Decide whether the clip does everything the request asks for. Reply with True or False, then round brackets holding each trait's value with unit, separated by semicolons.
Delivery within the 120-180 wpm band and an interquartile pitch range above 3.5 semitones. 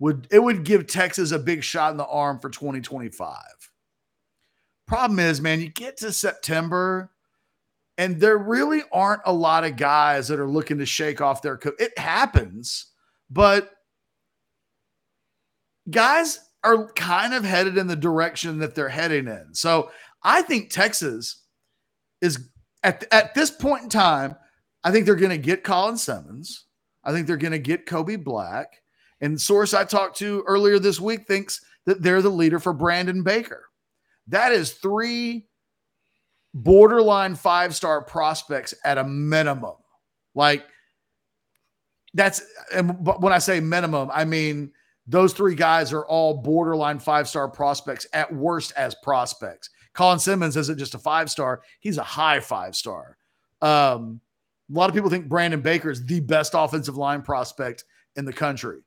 True (155 wpm; 4.7 semitones)